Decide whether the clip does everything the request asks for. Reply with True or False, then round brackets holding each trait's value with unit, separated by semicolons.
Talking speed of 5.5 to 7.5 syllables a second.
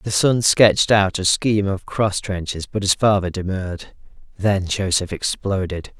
False (4.5 syllables/s)